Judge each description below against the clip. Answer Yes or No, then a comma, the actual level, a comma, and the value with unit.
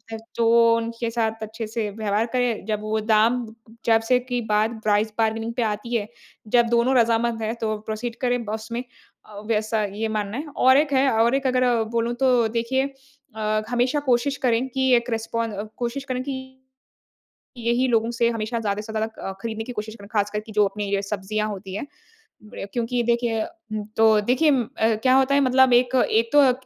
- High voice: Yes, high, 230 Hz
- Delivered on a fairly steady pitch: Yes, narrow, 2.2 semitones